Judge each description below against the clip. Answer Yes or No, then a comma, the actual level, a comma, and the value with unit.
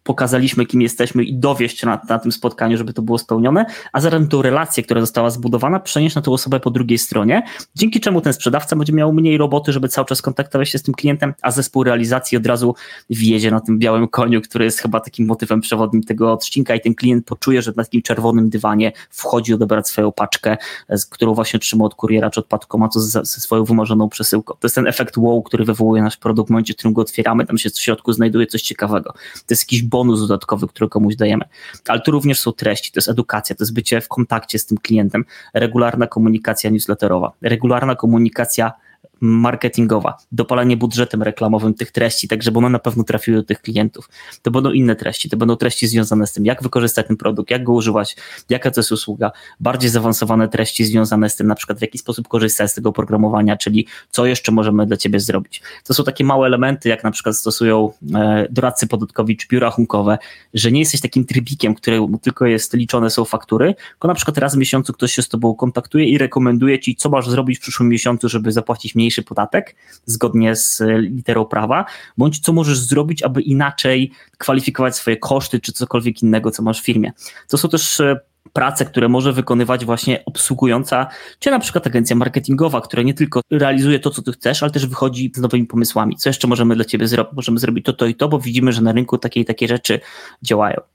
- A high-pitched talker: No, low, 120 Hz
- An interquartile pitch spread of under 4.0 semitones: Yes, narrow, 2.6 semitones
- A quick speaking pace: Yes, fast, 210 wpm